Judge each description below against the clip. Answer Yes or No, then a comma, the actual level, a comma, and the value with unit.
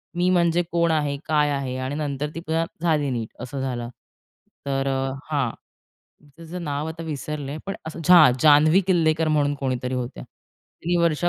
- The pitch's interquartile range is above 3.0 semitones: Yes, average, 3.4 semitones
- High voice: No, medium, 150 Hz